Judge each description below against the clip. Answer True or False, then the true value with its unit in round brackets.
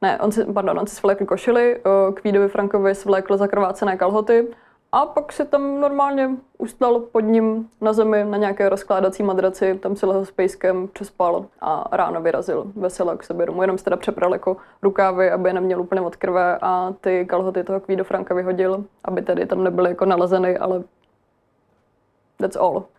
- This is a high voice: True (195 Hz)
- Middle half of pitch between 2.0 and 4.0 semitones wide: True (2.5 semitones)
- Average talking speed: False (175 wpm)